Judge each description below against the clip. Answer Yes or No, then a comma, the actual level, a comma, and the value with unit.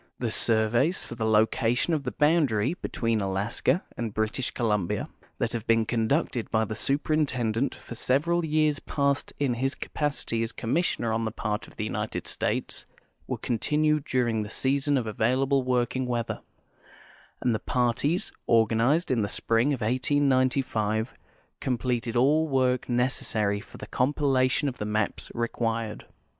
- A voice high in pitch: No, low, 120 Hz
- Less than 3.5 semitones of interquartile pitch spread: No, average, 3.8 semitones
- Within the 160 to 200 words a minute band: No, average, 150 wpm